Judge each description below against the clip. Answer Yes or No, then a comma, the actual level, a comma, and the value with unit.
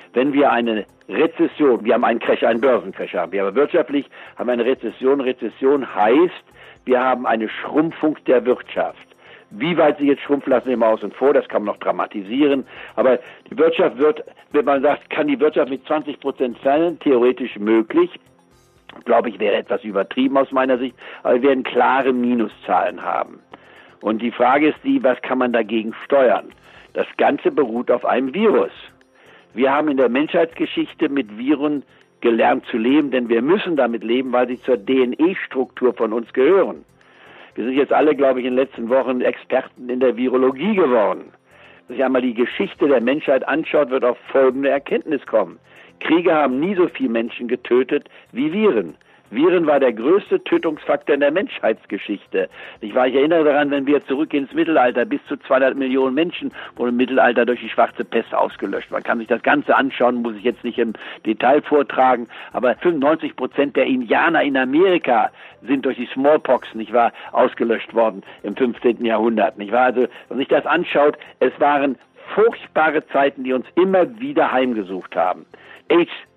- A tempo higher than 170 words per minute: Yes, average, 180 wpm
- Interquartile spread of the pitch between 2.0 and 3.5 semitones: No, average, 4.0 semitones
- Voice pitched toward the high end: No, low, 130 Hz